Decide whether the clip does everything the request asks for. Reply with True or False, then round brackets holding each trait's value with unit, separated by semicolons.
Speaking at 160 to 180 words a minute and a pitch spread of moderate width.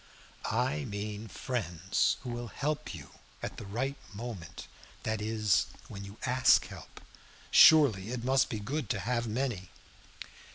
False (140 wpm; 3.9 semitones)